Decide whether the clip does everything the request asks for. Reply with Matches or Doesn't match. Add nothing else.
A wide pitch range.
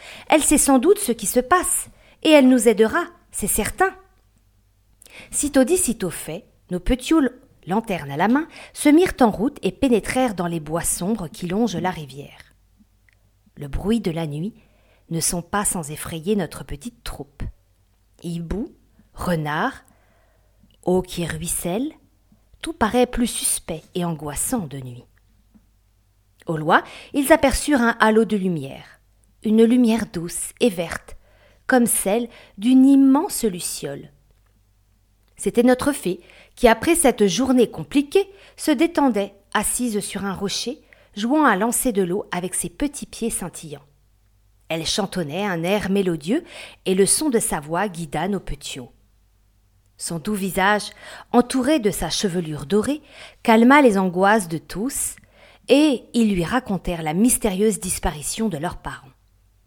Matches